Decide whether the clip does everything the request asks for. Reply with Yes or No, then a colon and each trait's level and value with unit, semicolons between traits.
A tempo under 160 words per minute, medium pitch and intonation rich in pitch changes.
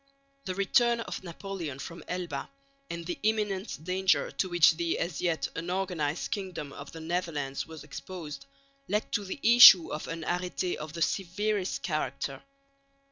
No: average, 150 wpm; medium, 175 Hz; average, 3.5 semitones